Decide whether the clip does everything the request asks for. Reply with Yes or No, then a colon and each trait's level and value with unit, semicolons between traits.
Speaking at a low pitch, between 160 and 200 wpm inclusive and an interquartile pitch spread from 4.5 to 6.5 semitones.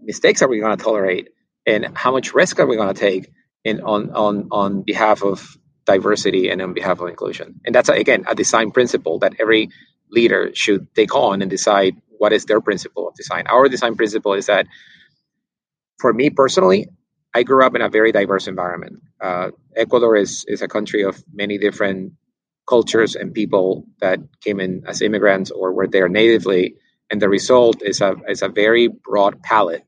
No: low, 105 Hz; average, 190 wpm; average, 3.2 semitones